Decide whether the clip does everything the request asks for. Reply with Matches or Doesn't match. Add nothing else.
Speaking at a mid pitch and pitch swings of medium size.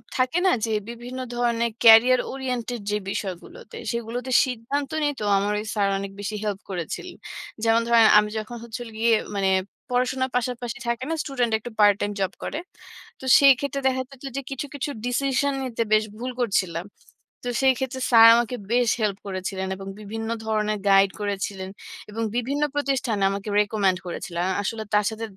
Doesn't match